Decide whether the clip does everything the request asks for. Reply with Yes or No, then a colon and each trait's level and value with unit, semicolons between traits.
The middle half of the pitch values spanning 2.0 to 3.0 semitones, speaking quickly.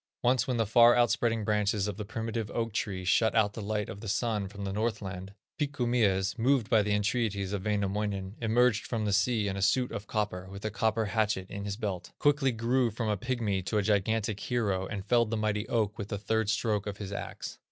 Yes: narrow, 2.4 semitones; fast, 220 wpm